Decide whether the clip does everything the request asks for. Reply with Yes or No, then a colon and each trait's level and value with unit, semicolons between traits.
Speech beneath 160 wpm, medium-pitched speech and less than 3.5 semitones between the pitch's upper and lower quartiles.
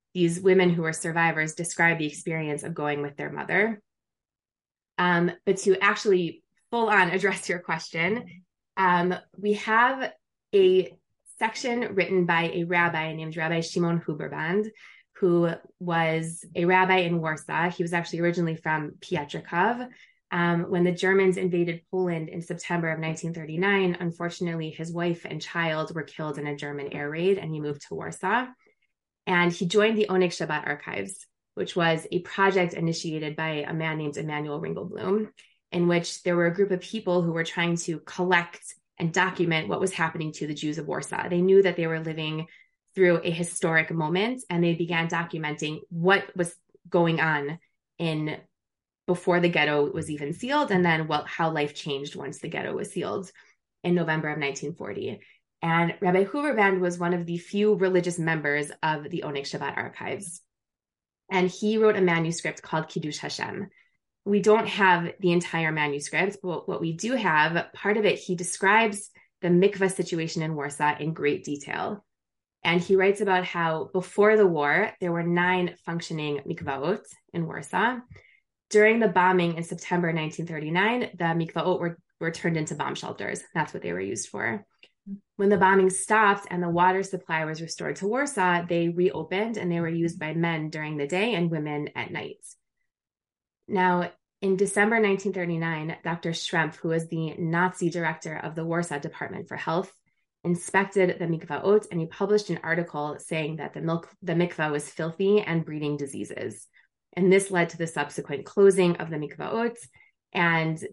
No: average, 170 wpm; medium, 175 Hz; average, 2.8 semitones